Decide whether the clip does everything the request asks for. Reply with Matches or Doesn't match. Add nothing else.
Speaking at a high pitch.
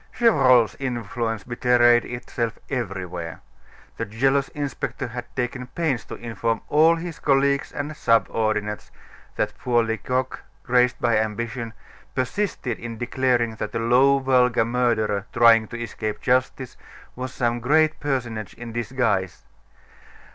Doesn't match